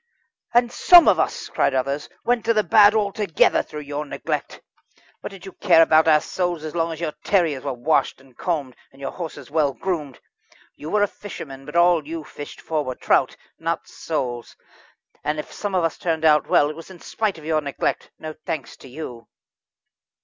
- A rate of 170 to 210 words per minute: Yes, average, 200 wpm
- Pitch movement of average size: Yes, average, 3.7 semitones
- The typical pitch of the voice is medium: Yes, medium, 160 Hz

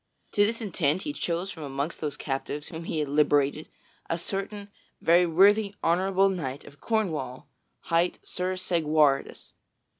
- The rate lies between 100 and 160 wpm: Yes, average, 145 wpm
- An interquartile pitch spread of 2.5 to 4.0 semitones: No, average, 4.6 semitones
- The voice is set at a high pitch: No, medium, 165 Hz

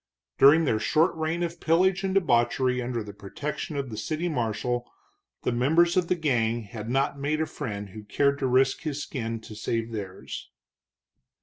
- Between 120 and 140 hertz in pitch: Yes, low, 135 Hz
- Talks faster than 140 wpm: Yes, average, 180 wpm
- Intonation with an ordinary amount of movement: No, wide, 5.7 semitones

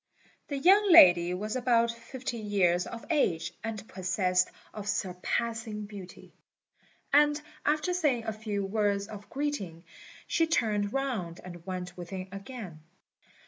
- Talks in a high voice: Yes, high, 210 Hz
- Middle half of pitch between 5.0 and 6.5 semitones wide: Yes, wide, 5.6 semitones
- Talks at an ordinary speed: No, slow, 130 wpm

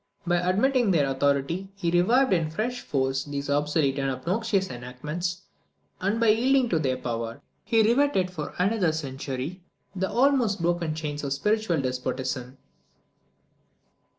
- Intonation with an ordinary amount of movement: No, wide, 7.0 semitones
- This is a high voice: No, medium, 170 Hz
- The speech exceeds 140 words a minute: No, slow, 135 wpm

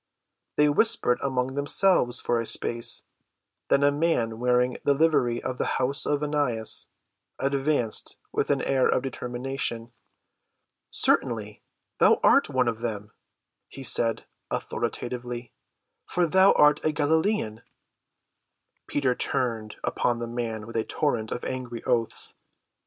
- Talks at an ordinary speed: No, slow, 130 wpm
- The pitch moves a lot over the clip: No, average, 3.4 semitones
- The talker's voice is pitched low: Yes, low, 125 Hz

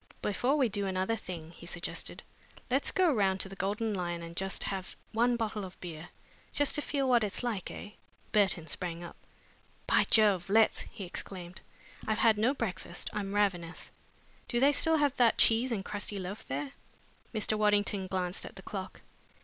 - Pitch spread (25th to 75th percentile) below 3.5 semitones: No, average, 3.8 semitones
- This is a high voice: Yes, high, 205 Hz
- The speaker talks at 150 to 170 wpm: No, average, 180 wpm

